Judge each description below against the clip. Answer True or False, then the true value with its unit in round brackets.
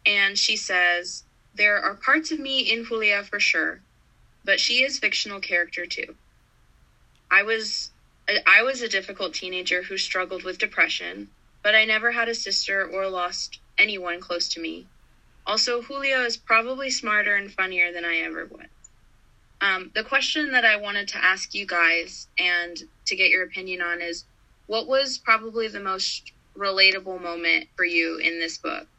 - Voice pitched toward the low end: False (195 Hz)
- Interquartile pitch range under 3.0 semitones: False (4.1 semitones)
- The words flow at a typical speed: True (170 wpm)